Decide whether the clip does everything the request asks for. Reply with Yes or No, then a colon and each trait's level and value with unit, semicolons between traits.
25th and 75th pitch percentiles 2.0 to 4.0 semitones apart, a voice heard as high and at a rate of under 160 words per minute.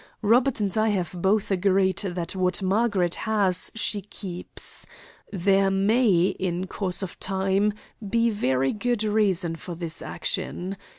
Yes: average, 2.7 semitones; high, 195 Hz; slow, 135 wpm